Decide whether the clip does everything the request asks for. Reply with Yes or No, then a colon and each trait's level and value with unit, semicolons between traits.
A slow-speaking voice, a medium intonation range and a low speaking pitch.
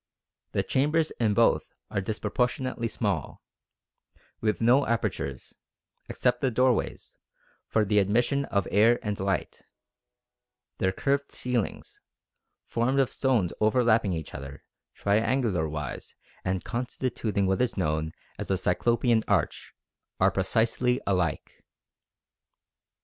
Yes: slow, 110 wpm; average, 4.4 semitones; low, 110 Hz